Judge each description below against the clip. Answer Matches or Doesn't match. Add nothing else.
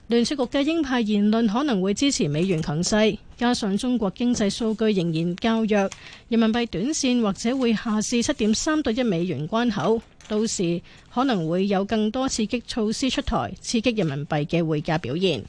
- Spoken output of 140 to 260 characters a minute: Doesn't match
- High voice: Matches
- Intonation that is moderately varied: Matches